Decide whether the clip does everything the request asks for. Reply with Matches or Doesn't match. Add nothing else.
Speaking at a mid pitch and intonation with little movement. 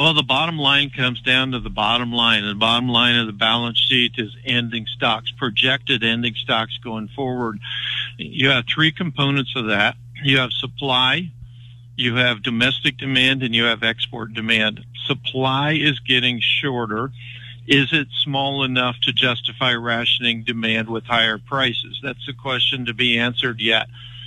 Doesn't match